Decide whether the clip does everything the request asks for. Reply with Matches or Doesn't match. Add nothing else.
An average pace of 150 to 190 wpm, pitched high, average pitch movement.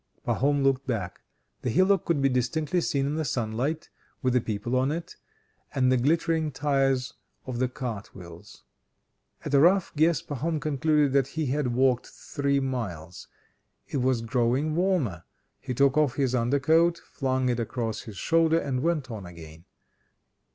Doesn't match